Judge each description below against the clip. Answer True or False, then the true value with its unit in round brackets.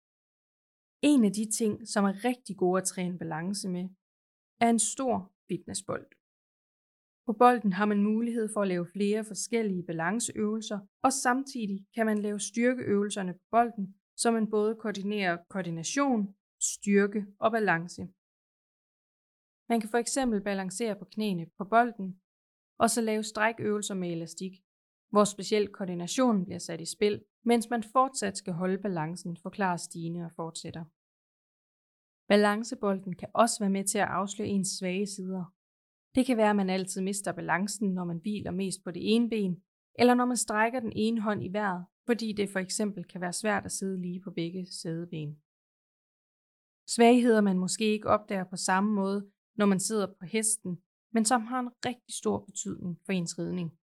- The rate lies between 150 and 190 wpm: True (165 wpm)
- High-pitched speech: True (200 Hz)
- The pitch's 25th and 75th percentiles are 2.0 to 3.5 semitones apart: True (3.1 semitones)